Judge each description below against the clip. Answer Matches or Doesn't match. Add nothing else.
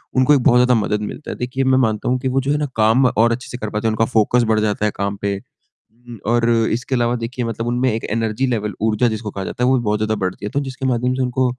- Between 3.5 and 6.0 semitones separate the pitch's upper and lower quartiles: Doesn't match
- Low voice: Matches